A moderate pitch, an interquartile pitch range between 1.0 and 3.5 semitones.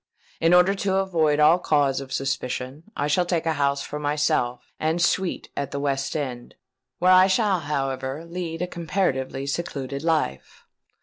No: medium, 150 Hz; average, 4.1 semitones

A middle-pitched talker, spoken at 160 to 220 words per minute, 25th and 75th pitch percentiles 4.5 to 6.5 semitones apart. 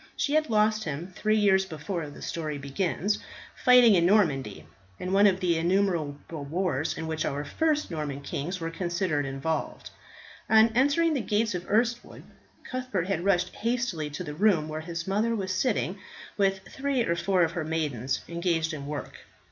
Yes: medium, 180 Hz; average, 170 wpm; average, 5.2 semitones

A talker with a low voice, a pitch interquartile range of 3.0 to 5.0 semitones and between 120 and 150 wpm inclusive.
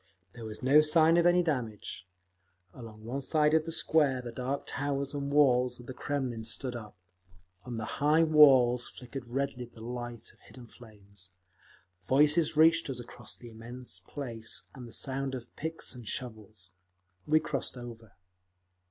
No: low, 125 Hz; average, 3.9 semitones; average, 160 wpm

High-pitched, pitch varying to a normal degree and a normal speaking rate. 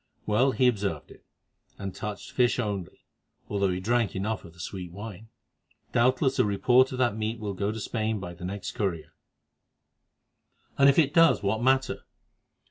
No: low, 110 Hz; average, 4.0 semitones; average, 170 wpm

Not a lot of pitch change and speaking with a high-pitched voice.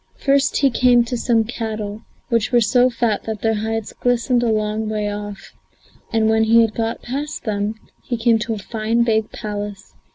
Yes: narrow, 1.9 semitones; high, 225 Hz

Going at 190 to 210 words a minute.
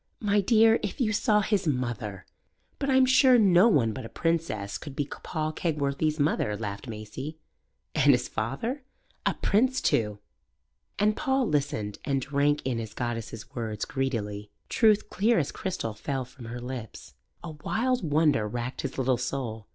No: average, 160 wpm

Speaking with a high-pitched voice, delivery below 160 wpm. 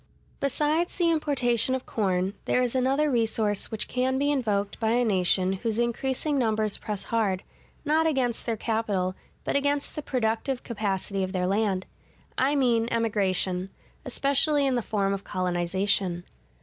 Yes: high, 225 Hz; average, 150 wpm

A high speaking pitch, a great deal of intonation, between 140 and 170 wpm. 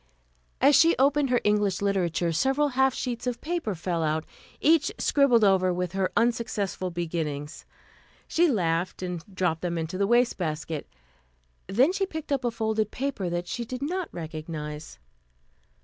Yes: high, 200 Hz; wide, 7.4 semitones; average, 150 wpm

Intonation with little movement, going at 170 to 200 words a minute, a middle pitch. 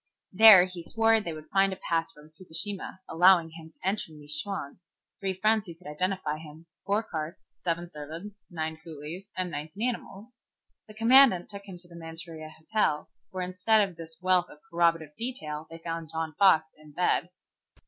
No: average, 3.6 semitones; average, 180 wpm; medium, 175 Hz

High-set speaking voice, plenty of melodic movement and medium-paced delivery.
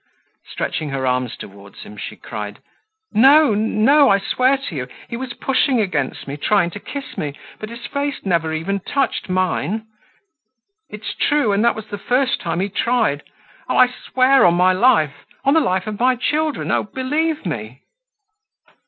Yes: high, 210 Hz; wide, 8.1 semitones; average, 170 wpm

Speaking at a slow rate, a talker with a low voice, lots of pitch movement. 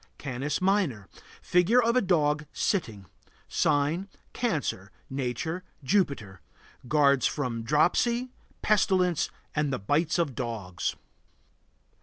No: slow, 100 wpm; medium, 150 Hz; wide, 6.6 semitones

